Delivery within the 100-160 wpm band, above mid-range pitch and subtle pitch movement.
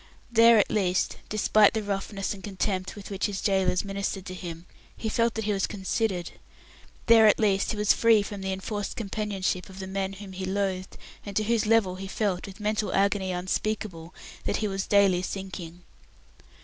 No: average, 190 wpm; high, 195 Hz; narrow, 2.0 semitones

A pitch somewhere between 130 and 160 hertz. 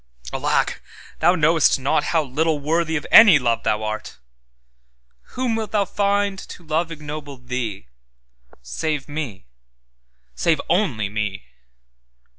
Yes: medium, 140 Hz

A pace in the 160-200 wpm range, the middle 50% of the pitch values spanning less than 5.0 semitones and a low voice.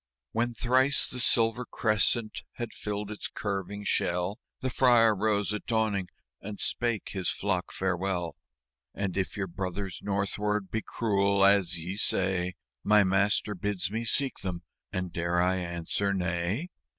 No: average, 150 wpm; average, 2.7 semitones; low, 100 Hz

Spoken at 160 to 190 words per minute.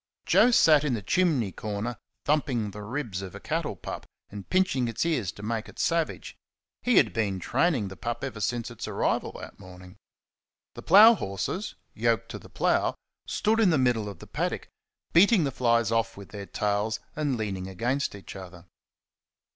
Yes: average, 180 wpm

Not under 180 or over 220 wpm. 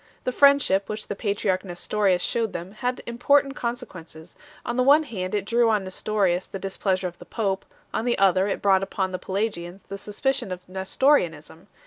Yes: average, 185 wpm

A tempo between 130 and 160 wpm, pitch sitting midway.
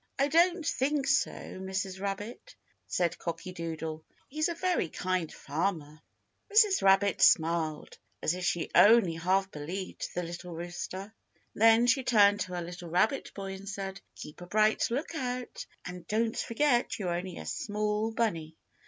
No: average, 155 wpm; high, 195 Hz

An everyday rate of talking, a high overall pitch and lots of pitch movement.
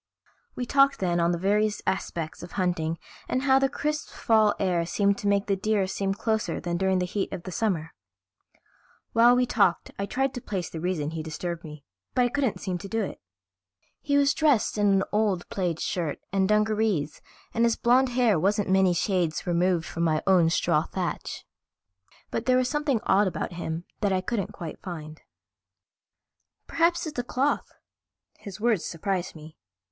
No: average, 180 wpm; high, 195 Hz; average, 5.0 semitones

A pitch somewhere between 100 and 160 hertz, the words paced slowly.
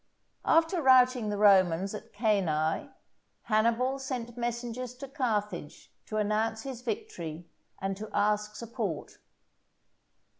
No: high, 220 Hz; slow, 110 wpm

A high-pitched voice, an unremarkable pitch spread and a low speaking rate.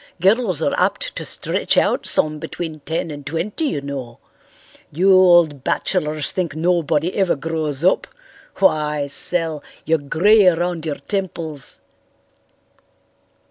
No: medium, 160 Hz; average, 3.3 semitones; slow, 125 wpm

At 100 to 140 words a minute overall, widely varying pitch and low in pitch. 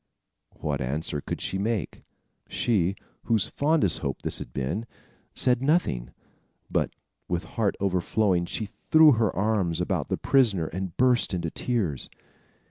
Yes: slow, 135 wpm; wide, 5.7 semitones; low, 100 Hz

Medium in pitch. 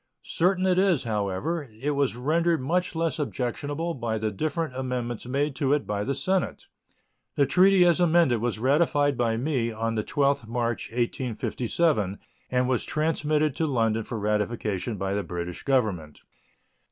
No: low, 130 Hz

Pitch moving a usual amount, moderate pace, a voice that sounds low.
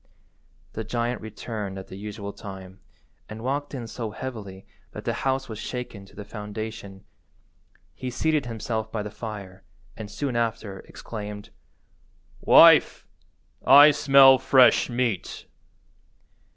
No: average, 3.5 semitones; slow, 125 wpm; low, 110 Hz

